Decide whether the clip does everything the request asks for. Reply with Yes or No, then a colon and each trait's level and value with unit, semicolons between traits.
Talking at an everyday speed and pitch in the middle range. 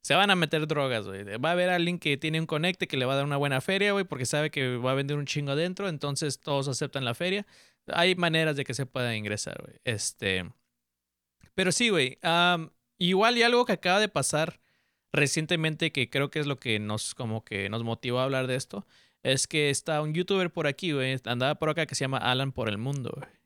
No: fast, 230 wpm; medium, 145 Hz